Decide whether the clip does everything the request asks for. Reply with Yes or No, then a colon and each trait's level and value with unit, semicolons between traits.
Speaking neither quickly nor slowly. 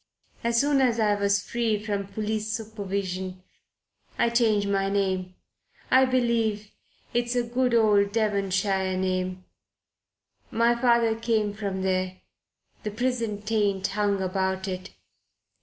No: slow, 125 wpm